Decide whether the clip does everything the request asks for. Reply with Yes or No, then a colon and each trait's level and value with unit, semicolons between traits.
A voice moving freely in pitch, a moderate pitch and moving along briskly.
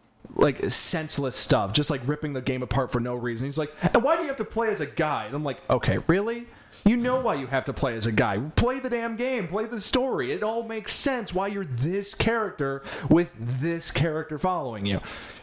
Yes: wide, 8.5 semitones; medium, 160 Hz; fast, 230 wpm